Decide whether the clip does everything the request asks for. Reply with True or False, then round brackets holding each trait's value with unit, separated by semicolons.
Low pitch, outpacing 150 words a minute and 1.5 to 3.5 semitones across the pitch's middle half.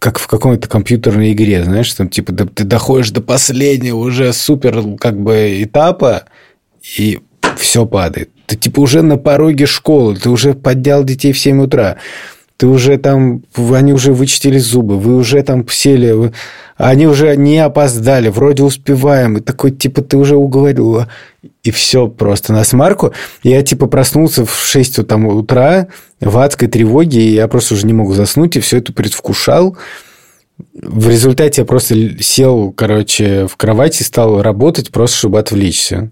False (125 Hz; 160 wpm; 4.1 semitones)